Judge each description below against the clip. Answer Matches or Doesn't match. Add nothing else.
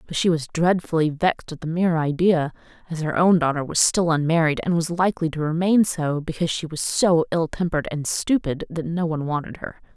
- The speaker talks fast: Matches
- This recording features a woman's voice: Matches